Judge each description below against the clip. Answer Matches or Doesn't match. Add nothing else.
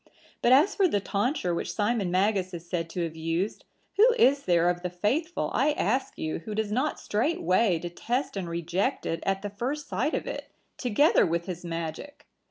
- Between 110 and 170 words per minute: Doesn't match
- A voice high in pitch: Matches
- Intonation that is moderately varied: Doesn't match